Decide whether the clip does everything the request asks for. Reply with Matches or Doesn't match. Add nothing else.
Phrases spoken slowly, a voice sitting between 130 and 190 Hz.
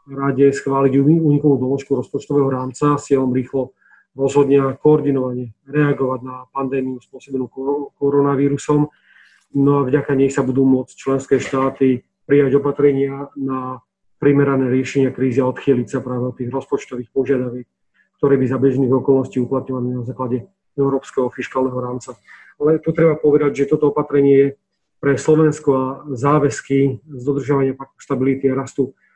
Doesn't match